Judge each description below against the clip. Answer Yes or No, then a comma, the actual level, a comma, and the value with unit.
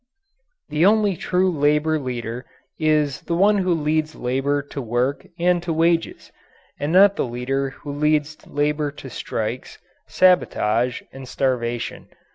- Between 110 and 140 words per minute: Yes, slow, 135 wpm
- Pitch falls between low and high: Yes, medium, 150 Hz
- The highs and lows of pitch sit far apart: No, average, 4.2 semitones